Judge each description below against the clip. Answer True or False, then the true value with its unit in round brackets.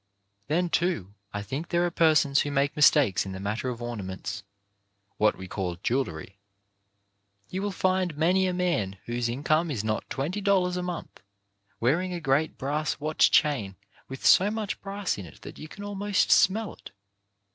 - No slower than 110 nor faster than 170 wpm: False (180 wpm)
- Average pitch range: False (8.9 semitones)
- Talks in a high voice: False (150 Hz)